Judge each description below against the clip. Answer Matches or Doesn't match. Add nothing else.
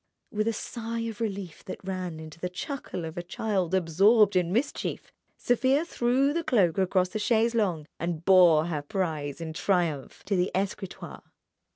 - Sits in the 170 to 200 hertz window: Matches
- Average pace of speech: Matches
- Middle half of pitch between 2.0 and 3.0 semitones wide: Doesn't match